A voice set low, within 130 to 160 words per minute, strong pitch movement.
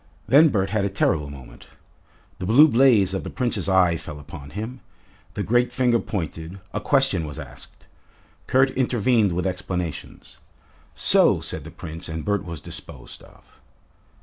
Yes: very low, 95 Hz; average, 155 wpm; wide, 6.6 semitones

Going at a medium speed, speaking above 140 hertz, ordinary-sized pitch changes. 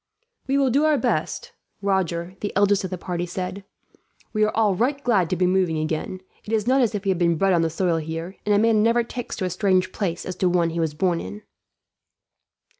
No: fast, 235 wpm; high, 190 Hz; average, 3.8 semitones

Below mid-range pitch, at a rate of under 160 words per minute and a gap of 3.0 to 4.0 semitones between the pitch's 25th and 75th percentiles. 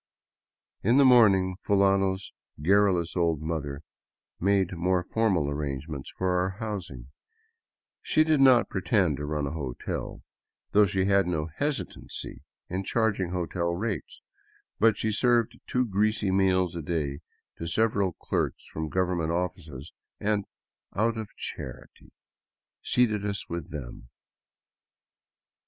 No: very low, 95 Hz; slow, 135 wpm; average, 4.5 semitones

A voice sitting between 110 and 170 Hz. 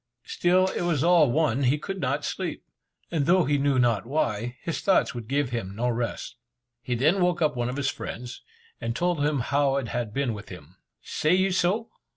Yes: medium, 140 Hz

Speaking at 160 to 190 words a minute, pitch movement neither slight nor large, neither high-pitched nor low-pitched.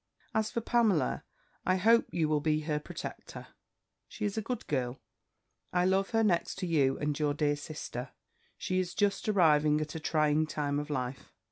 Yes: average, 180 wpm; average, 4.8 semitones; medium, 155 Hz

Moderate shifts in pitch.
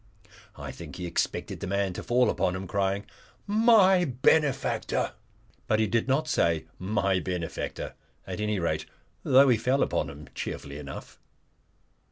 No: wide, 6.7 semitones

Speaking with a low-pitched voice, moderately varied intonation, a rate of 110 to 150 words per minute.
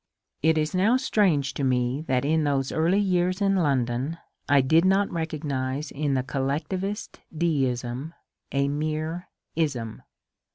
No: medium, 150 Hz; average, 4.3 semitones; average, 140 wpm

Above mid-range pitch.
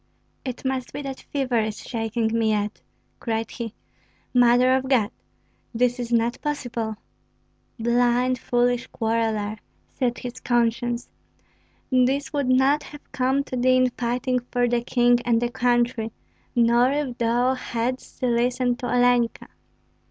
Yes: high, 245 Hz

